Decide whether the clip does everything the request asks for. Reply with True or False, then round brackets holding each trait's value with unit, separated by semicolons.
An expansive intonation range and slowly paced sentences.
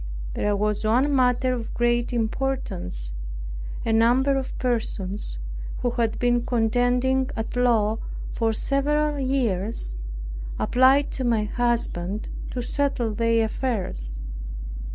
False (3.1 semitones; 110 wpm)